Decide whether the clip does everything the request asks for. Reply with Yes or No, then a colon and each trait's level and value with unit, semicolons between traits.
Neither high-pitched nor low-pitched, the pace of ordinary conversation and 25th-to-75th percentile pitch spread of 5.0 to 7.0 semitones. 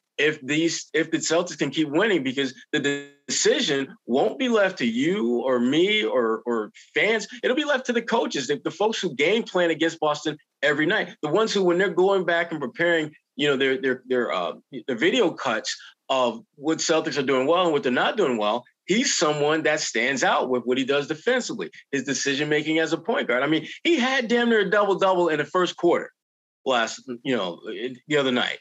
No: medium, 160 Hz; fast, 215 wpm; average, 5.3 semitones